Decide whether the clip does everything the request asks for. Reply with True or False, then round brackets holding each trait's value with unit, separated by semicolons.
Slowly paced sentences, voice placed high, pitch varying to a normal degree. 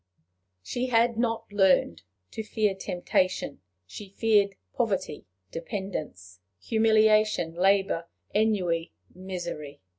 True (90 wpm; 195 Hz; 4.3 semitones)